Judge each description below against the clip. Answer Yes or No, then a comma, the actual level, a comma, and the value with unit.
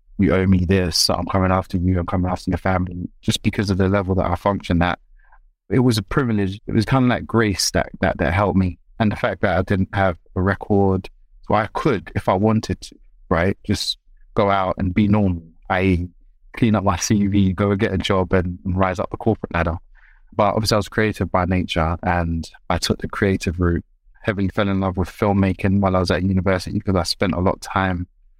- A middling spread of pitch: No, narrow, 2.1 semitones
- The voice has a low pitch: Yes, very low, 95 Hz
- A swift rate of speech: Yes, fast, 230 wpm